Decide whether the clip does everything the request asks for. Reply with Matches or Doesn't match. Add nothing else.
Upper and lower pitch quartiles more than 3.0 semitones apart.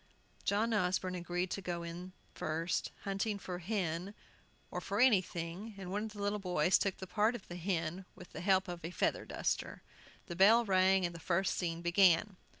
Doesn't match